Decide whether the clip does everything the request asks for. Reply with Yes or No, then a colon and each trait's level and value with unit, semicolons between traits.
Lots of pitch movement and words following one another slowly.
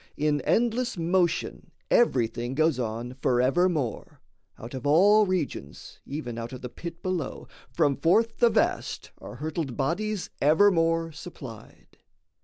Yes: wide, 6.3 semitones; slow, 125 wpm